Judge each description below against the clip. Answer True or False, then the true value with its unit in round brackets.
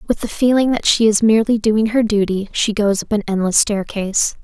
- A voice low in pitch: False (215 Hz)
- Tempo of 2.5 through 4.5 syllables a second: False (5.5 syllables/s)